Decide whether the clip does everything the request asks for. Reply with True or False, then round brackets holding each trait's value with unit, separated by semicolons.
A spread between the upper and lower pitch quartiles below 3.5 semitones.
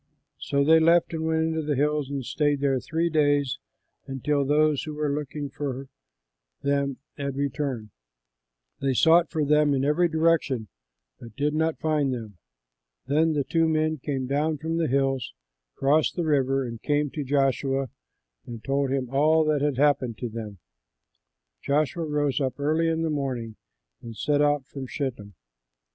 True (2.4 semitones)